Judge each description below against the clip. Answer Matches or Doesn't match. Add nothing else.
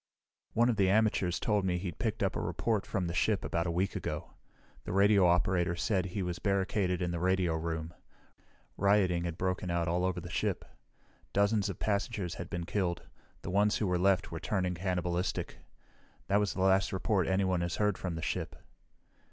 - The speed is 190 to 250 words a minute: Matches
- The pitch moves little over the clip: Matches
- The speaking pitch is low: Matches